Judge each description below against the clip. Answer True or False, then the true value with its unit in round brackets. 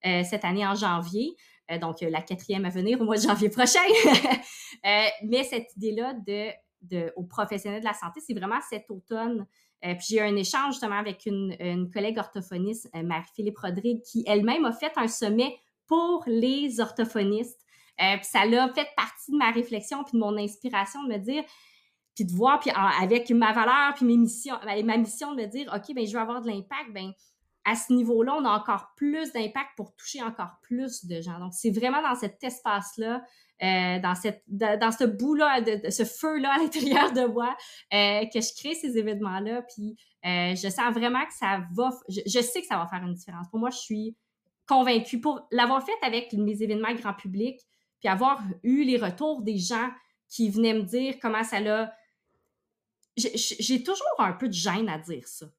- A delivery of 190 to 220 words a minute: True (195 wpm)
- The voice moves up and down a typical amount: True (3.8 semitones)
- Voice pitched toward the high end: True (225 Hz)